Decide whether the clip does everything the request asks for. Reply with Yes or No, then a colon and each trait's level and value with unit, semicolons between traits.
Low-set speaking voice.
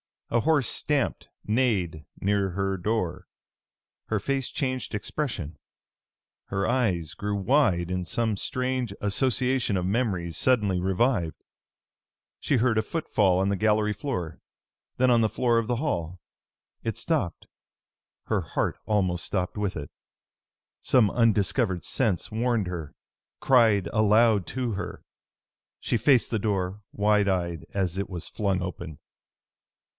Yes: low, 105 Hz